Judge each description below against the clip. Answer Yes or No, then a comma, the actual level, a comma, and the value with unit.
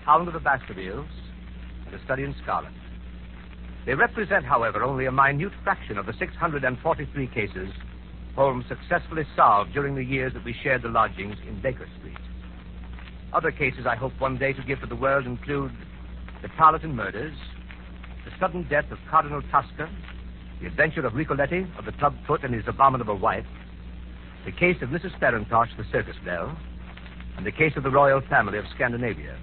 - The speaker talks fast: No, average, 175 wpm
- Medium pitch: No, low, 120 Hz